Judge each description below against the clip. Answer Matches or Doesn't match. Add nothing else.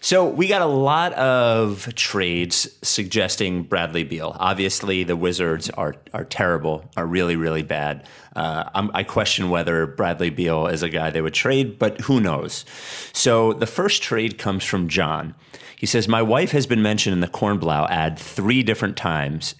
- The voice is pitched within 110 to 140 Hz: Doesn't match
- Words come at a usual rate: Matches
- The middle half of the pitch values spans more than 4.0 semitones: Matches